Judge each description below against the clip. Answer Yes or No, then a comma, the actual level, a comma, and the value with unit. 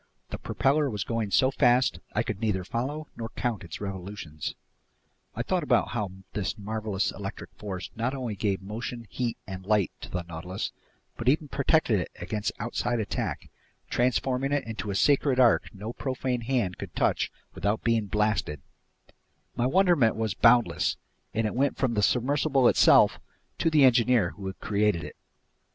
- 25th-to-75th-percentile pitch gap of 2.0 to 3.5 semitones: No, average, 4.0 semitones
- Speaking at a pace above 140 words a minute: Yes, average, 165 wpm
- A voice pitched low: Yes, low, 115 Hz